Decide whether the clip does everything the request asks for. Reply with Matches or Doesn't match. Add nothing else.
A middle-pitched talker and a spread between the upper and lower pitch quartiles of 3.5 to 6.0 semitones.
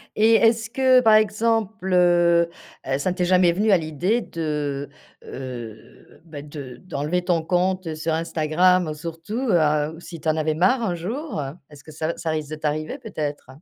Matches